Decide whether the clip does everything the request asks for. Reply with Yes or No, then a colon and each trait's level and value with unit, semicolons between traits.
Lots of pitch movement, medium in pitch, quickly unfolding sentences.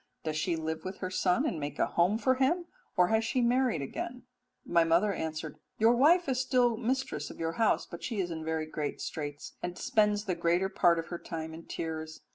Yes: wide, 6.4 semitones; medium, 180 Hz; fast, 220 wpm